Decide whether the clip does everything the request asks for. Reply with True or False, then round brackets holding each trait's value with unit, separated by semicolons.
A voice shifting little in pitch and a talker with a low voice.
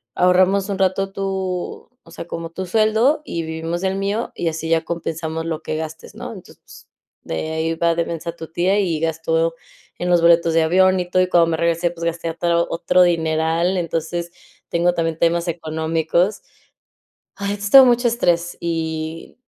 False (2.2 semitones; 170 Hz)